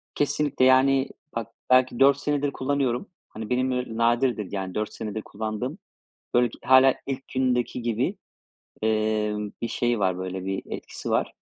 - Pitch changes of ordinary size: Yes, average, 3.4 semitones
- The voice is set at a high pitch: No, low, 120 Hz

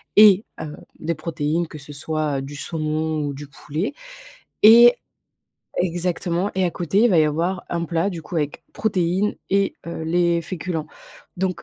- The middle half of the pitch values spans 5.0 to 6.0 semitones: No, average, 3.1 semitones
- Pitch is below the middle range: No, medium, 170 Hz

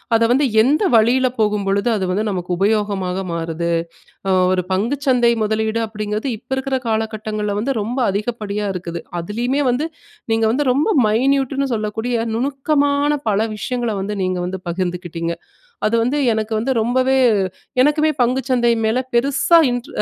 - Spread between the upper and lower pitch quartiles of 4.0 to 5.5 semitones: Yes, average, 4.3 semitones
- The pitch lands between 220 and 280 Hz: Yes, high, 225 Hz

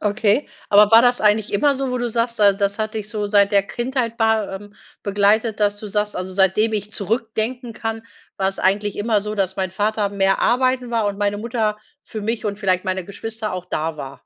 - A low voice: No, high, 210 Hz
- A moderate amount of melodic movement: No, narrow, 2.1 semitones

